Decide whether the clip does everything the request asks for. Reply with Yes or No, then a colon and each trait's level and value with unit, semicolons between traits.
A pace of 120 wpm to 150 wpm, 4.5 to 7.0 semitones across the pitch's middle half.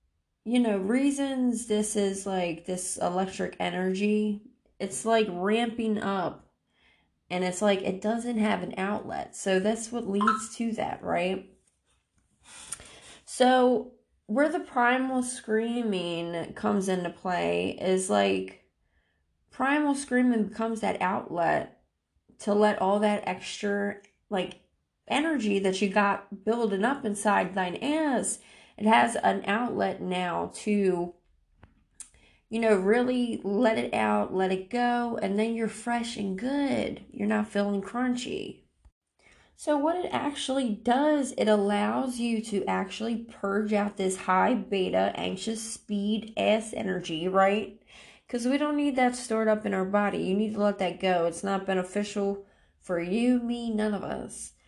No: average, 140 wpm; average, 3.7 semitones